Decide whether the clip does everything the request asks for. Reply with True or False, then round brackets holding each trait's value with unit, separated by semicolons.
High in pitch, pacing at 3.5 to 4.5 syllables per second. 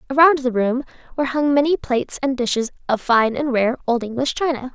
False (260 Hz; 5.8 syllables/s)